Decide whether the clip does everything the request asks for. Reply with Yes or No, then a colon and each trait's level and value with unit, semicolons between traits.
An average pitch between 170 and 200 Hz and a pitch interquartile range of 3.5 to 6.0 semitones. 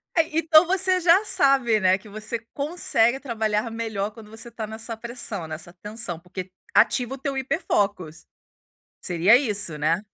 No: high, 225 Hz; average, 5.3 semitones